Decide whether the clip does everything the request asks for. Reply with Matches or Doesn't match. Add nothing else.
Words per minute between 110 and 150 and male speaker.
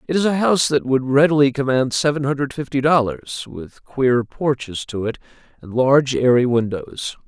Doesn't match